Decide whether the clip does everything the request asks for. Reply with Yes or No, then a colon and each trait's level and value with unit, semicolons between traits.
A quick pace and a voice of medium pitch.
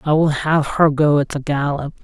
Yes: fast, 235 wpm; medium, 150 Hz